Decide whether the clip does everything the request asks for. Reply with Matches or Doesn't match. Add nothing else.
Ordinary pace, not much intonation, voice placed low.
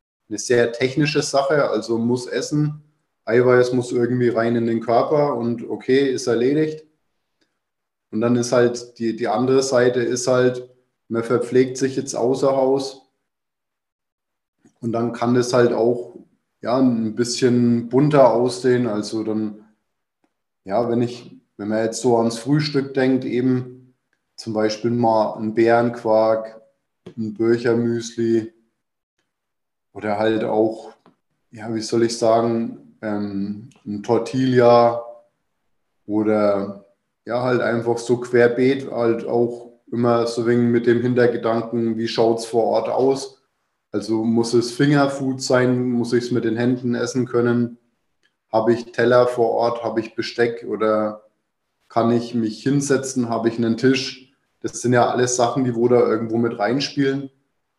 Matches